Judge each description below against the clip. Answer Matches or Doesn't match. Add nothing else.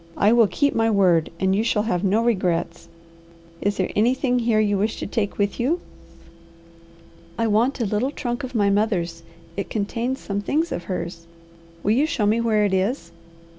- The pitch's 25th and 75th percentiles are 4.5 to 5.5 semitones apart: Doesn't match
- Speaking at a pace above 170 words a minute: Matches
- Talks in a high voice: Matches